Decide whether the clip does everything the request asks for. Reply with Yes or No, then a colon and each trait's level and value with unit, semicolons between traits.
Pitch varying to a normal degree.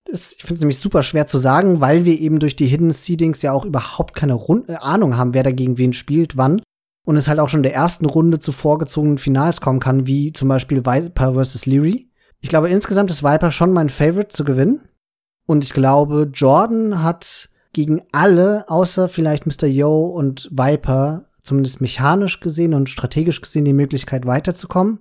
Yes: average, 3.8 semitones